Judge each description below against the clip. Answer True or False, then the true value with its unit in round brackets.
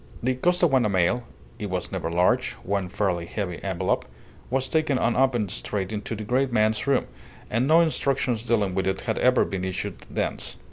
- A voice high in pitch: False (110 Hz)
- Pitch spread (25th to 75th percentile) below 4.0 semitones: False (5.1 semitones)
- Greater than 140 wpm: True (175 wpm)